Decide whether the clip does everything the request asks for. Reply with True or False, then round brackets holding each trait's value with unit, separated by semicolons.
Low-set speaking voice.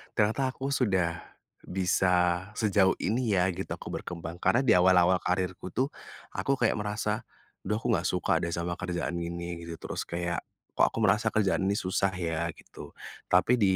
True (95 Hz)